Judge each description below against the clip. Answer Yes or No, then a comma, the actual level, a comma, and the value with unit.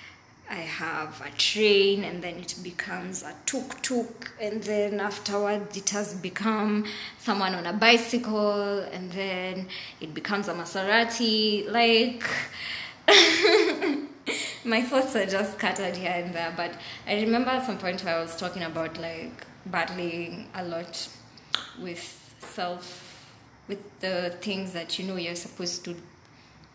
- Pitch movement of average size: Yes, average, 3.4 semitones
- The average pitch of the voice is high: Yes, high, 195 Hz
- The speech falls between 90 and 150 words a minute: Yes, slow, 135 wpm